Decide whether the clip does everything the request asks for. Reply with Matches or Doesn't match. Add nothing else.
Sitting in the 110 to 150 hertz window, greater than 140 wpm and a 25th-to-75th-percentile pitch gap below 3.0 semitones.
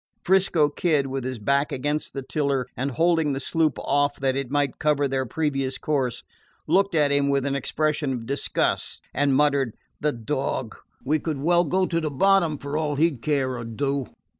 Matches